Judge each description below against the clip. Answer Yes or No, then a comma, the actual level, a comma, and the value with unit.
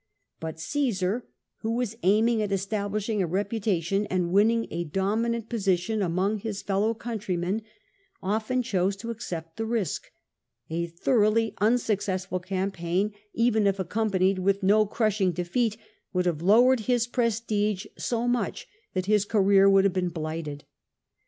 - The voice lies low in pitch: No, high, 200 Hz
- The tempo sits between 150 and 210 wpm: No, average, 140 wpm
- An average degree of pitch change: Yes, average, 3.4 semitones